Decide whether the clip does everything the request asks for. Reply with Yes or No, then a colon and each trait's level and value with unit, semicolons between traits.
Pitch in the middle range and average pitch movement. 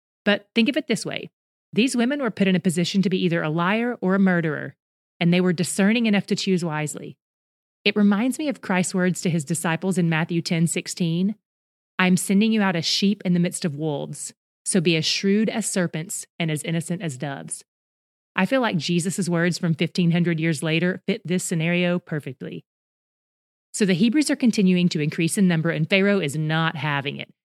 Yes: medium, 180 Hz; average, 3.1 semitones